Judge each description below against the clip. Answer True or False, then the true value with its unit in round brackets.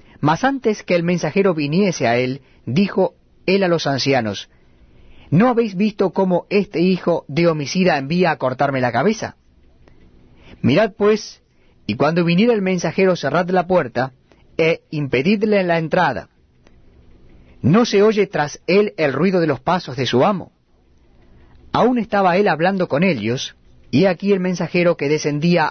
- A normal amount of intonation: False (7.0 semitones)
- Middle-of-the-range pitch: True (170 Hz)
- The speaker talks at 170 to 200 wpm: False (150 wpm)